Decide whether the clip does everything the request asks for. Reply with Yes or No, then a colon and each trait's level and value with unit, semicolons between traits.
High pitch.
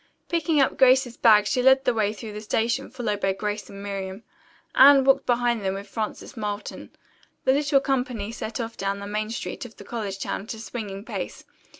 Yes: high, 225 Hz